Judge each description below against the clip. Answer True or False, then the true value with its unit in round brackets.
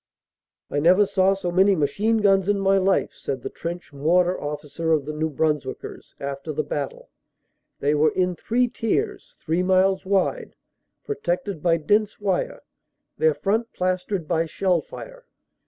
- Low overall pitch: False (185 Hz)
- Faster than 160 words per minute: False (155 wpm)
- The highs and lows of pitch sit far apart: False (4.4 semitones)